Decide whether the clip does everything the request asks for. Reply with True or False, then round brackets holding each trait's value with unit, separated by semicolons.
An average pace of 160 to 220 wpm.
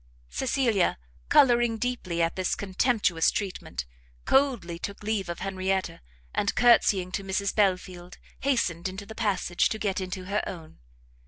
False (140 wpm)